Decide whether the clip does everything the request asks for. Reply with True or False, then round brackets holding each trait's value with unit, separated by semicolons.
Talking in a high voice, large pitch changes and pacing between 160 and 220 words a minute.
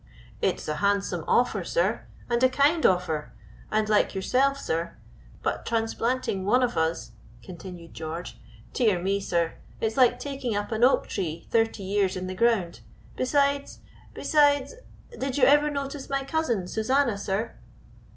False (225 Hz; 6.3 semitones; 150 wpm)